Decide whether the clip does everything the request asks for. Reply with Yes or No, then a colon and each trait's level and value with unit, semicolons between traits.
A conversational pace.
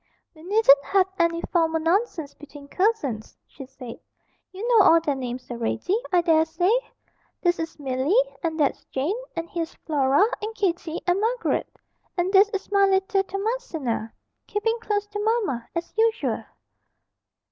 Yes: average, 150 wpm